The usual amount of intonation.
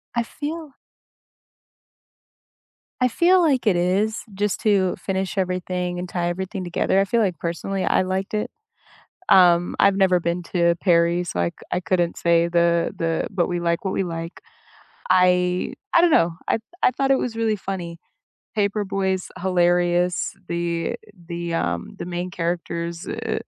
No: narrow, 2.3 semitones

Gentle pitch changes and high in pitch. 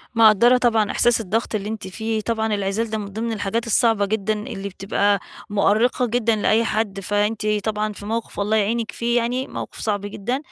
Yes: narrow, 2.0 semitones; high, 220 Hz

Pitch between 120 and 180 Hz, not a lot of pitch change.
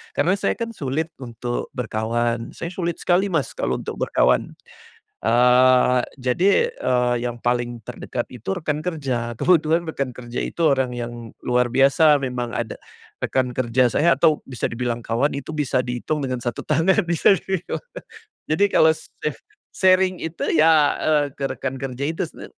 No: low, 135 Hz; average, 4.8 semitones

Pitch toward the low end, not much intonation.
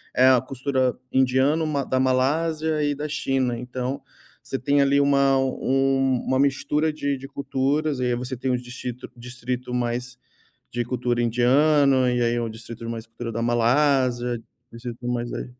Yes: low, 130 Hz; narrow, 2.3 semitones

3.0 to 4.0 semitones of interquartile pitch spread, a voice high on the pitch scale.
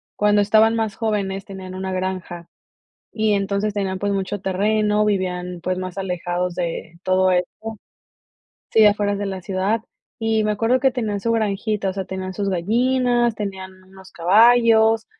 No: narrow, 2.6 semitones; high, 200 Hz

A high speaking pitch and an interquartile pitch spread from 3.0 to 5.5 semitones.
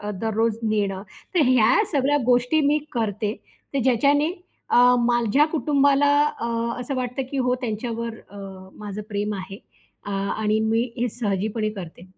Yes: high, 230 Hz; average, 3.6 semitones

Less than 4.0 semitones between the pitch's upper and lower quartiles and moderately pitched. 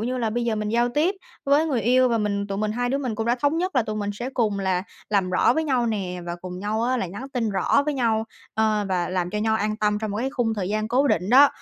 No: average, 3.6 semitones; high, 220 Hz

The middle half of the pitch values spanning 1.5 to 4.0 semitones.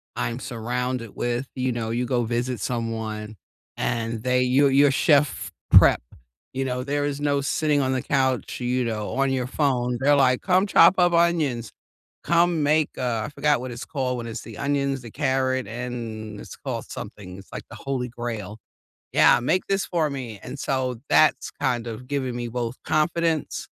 Yes: average, 3.2 semitones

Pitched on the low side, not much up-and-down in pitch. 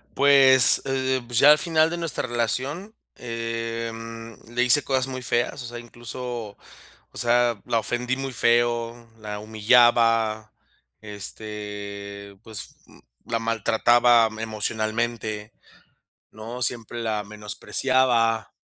Yes: low, 115 Hz; narrow, 2.2 semitones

